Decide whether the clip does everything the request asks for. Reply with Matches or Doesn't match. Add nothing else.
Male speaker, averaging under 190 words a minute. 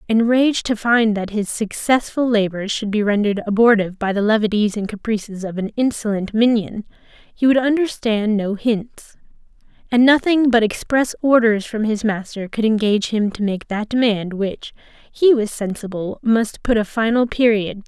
Doesn't match